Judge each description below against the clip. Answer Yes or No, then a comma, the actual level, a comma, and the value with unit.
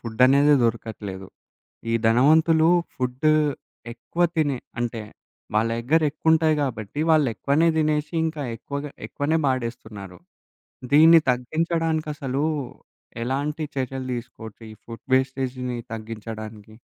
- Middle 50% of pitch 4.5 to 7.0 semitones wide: Yes, average, 5.0 semitones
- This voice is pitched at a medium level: No, low, 130 Hz